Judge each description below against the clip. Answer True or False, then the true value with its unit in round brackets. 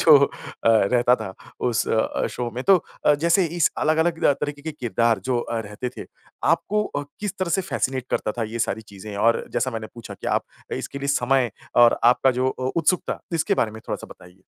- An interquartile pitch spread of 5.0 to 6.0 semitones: True (5.4 semitones)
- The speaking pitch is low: True (130 Hz)